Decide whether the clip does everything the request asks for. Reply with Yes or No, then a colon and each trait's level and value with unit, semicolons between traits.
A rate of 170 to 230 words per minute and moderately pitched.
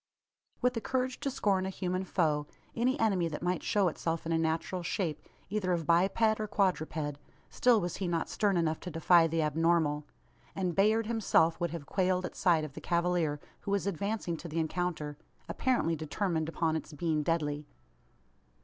Yes: average, 180 wpm; medium, 175 Hz